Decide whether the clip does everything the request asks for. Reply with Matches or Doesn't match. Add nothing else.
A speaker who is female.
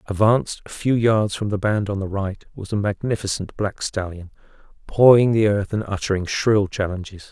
Doesn't match